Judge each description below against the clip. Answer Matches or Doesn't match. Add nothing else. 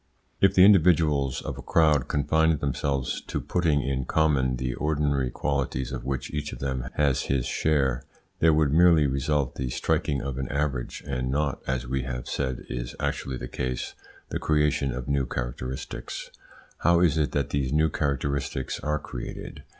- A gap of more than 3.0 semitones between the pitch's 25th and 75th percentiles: Doesn't match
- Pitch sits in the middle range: Doesn't match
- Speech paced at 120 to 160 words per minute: Doesn't match